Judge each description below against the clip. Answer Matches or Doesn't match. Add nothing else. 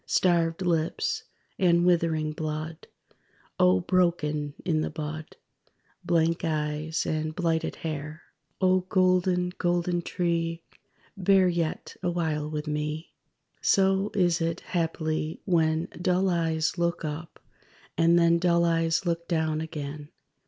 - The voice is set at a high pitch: Doesn't match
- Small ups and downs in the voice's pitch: Matches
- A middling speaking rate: Doesn't match